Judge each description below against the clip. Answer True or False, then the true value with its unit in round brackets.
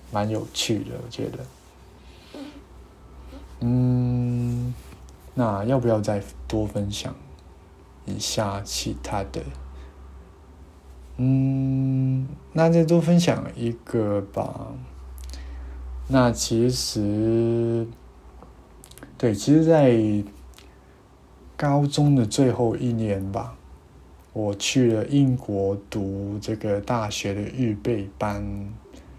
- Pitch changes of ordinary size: False (7.2 semitones)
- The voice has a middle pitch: False (105 Hz)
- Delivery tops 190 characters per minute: False (120 characters per minute)